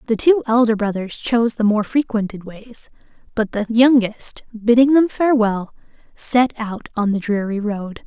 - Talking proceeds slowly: No, average, 155 wpm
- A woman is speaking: Yes, female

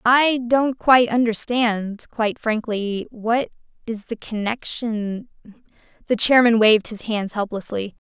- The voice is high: Yes, high, 225 Hz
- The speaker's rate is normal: No, slow, 120 wpm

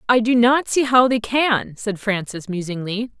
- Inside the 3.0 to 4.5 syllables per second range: Yes, 4.4 syllables/s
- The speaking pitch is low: No, high, 225 Hz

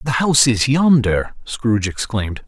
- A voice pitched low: Yes, low, 125 Hz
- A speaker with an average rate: Yes, average, 145 wpm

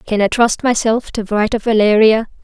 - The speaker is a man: No, female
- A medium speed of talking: Yes, average, 195 wpm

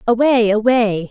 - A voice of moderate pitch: No, high, 225 Hz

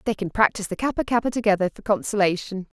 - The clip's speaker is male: No, female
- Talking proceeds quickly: No, average, 195 wpm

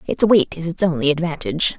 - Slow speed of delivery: No, average, 200 wpm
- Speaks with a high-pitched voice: No, medium, 165 Hz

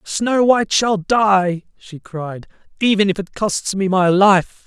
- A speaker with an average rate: Yes, average, 165 wpm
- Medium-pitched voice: No, high, 195 Hz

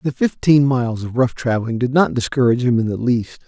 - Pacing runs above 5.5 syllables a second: Yes, 6.0 syllables/s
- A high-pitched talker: No, low, 120 Hz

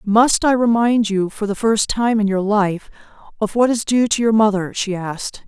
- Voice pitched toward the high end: Yes, high, 215 Hz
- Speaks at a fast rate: Yes, fast, 220 wpm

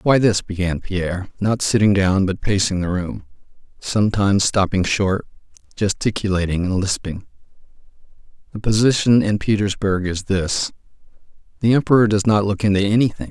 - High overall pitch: No, low, 100 Hz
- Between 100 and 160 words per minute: Yes, slow, 135 wpm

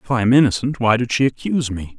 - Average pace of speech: No, fast, 275 wpm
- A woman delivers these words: No, male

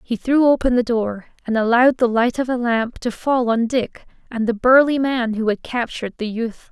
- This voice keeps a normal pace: No, fast, 225 wpm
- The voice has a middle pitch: No, high, 240 Hz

